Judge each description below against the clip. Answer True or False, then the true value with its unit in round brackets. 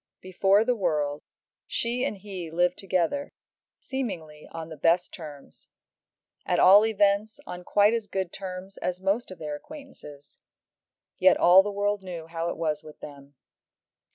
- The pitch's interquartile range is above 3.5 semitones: True (3.9 semitones)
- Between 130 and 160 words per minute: True (155 wpm)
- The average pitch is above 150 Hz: True (185 Hz)